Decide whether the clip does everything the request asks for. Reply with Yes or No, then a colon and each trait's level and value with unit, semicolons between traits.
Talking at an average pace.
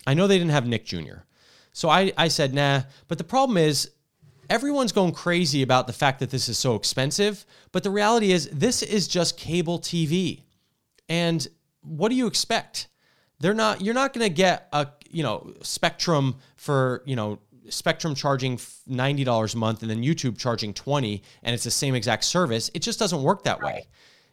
Yes: average, 185 wpm